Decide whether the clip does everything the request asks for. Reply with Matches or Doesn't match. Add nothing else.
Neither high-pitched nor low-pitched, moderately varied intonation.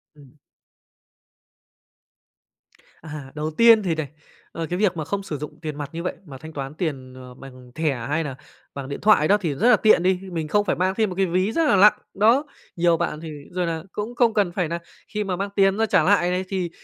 Matches